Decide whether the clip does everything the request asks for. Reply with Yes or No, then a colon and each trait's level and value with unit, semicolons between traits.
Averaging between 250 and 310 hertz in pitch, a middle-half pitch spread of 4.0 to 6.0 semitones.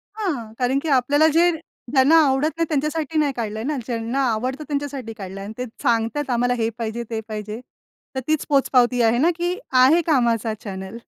Yes: very high, 255 Hz; average, 4.6 semitones